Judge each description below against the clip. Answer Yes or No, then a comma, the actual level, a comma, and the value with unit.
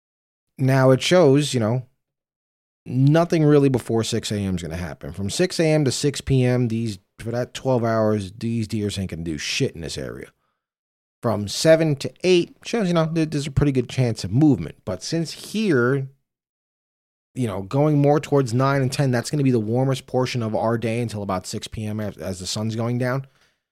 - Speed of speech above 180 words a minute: Yes, average, 200 wpm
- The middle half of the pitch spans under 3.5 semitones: No, average, 4.5 semitones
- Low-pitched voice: Yes, low, 125 Hz